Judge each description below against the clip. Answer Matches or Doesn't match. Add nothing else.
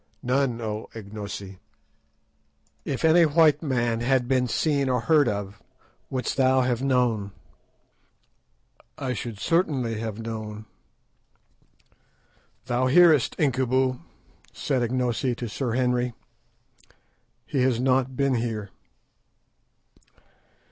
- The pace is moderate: Doesn't match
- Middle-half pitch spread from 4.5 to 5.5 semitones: Doesn't match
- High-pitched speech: Doesn't match